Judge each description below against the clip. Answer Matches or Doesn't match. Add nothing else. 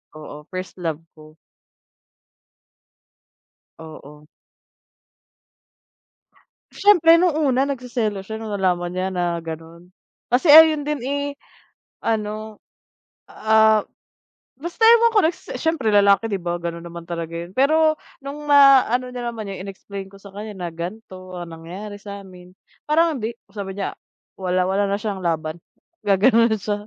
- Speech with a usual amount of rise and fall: Doesn't match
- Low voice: Doesn't match